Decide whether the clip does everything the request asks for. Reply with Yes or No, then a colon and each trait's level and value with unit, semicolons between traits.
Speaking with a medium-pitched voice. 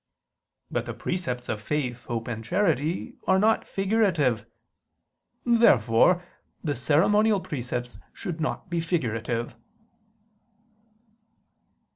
Yes: medium, 150 Hz